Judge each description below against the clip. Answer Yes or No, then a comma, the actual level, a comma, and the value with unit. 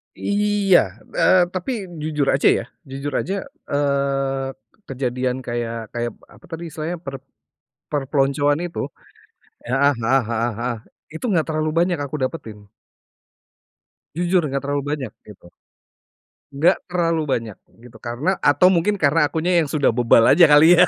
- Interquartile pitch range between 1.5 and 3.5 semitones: No, average, 4.3 semitones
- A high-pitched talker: No, medium, 145 Hz